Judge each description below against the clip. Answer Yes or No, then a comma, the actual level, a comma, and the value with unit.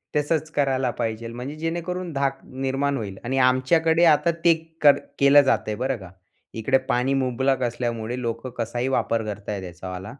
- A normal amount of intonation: Yes, average, 3.6 semitones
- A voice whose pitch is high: No, low, 130 Hz